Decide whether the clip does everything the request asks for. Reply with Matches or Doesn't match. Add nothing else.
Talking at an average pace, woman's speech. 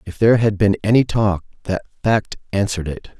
Doesn't match